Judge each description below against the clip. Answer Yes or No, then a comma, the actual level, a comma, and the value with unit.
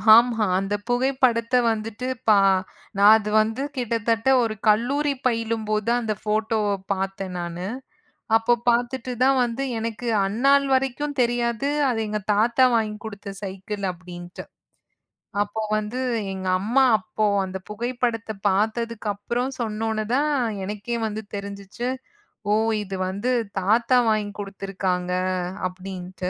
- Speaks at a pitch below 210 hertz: No, high, 220 Hz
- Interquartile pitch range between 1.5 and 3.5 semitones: Yes, average, 3.2 semitones